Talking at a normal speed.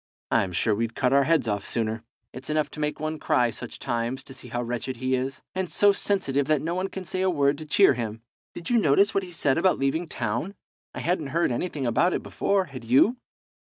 No: fast, 230 wpm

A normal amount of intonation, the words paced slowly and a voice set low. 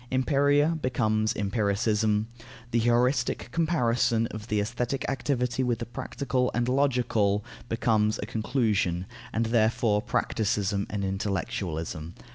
Yes: average, 3.1 semitones; slow, 110 wpm; low, 115 Hz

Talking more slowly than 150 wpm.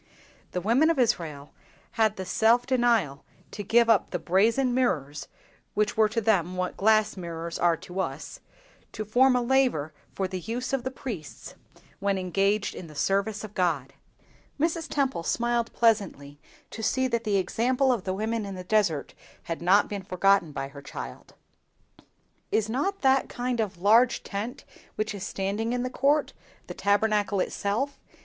No: average, 165 wpm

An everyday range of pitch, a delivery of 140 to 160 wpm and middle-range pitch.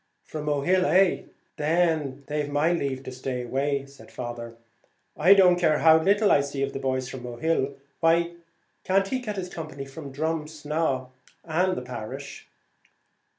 Yes: average, 3.9 semitones; average, 150 wpm; medium, 150 Hz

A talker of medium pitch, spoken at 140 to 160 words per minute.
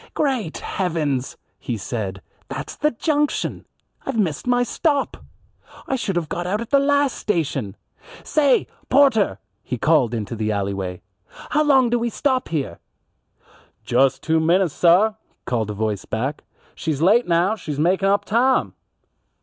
Yes: medium, 175 Hz; average, 150 wpm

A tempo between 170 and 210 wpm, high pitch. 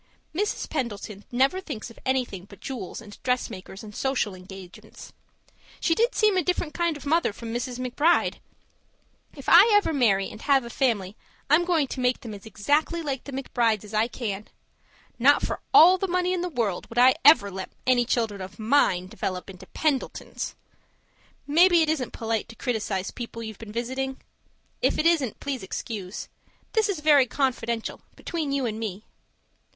Yes: average, 175 wpm; very high, 250 Hz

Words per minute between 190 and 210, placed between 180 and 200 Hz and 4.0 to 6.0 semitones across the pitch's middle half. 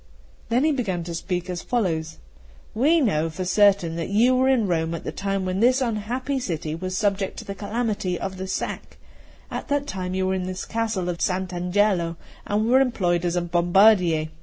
Yes: average, 195 wpm; high, 190 Hz; average, 4.3 semitones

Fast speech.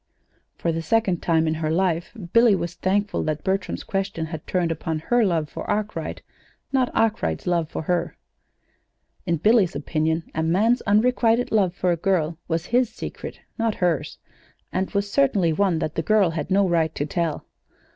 No: average, 175 wpm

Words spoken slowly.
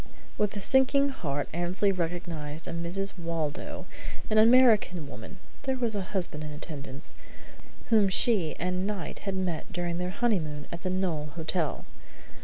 No: average, 150 wpm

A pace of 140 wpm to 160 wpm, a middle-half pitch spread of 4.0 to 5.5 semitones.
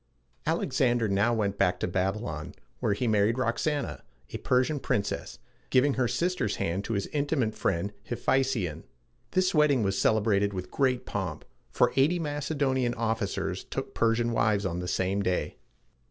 Yes: average, 155 wpm; average, 4.9 semitones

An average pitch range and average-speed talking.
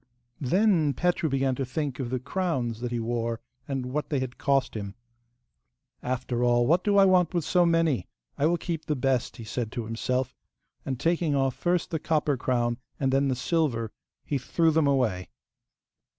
Yes: average, 4.8 semitones; average, 185 wpm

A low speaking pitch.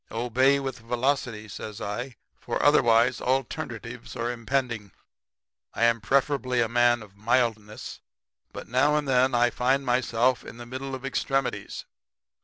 Yes: low, 120 Hz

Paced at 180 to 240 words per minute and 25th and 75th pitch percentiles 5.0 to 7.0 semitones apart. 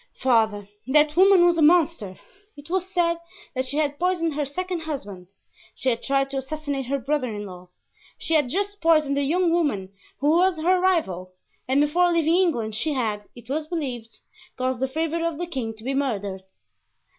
Yes: average, 190 wpm; wide, 5.4 semitones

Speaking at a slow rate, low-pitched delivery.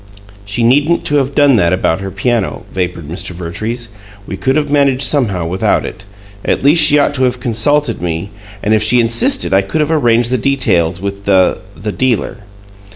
No: average, 190 wpm; low, 115 Hz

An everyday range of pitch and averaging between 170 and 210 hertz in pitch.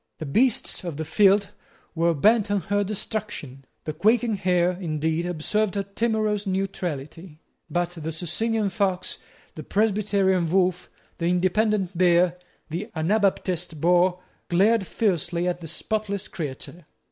Yes: average, 3.3 semitones; medium, 185 Hz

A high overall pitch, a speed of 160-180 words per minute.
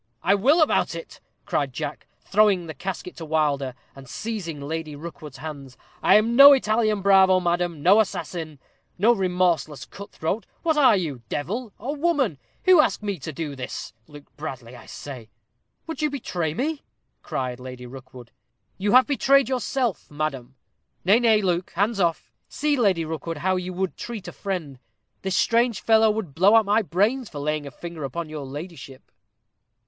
No: medium, 180 Hz; average, 170 wpm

